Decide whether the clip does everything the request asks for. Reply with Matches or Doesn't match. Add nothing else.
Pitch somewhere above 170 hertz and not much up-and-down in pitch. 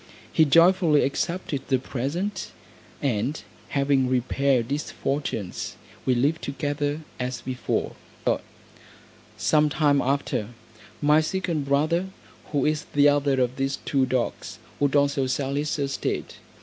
Doesn't match